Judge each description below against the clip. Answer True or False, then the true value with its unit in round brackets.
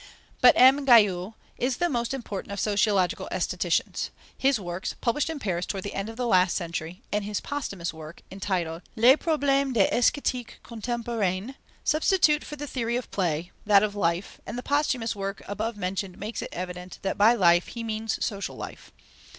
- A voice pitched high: True (210 Hz)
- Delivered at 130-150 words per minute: False (175 wpm)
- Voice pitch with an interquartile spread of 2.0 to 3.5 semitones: False (4.9 semitones)